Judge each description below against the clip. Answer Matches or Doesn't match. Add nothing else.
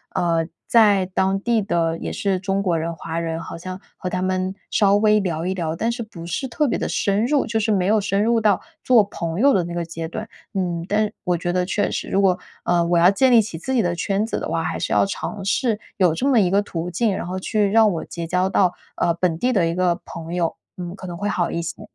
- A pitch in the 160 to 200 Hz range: Matches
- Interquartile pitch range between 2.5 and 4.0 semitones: Matches